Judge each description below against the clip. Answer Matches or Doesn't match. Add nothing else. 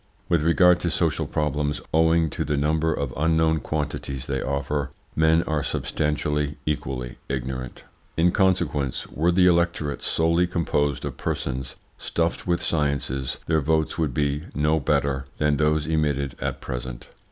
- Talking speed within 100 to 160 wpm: Matches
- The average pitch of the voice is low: Matches